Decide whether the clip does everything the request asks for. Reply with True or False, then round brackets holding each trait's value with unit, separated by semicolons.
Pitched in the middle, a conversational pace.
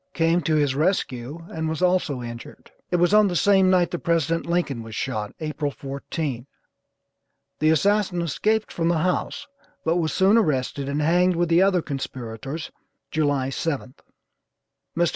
True (160 Hz; 160 wpm)